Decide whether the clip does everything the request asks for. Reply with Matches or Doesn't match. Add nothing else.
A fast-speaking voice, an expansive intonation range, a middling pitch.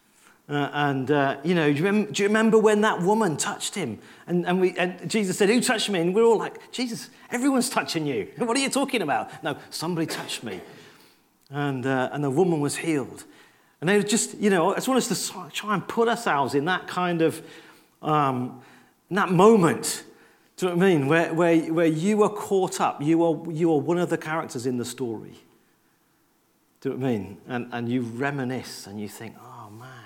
Matches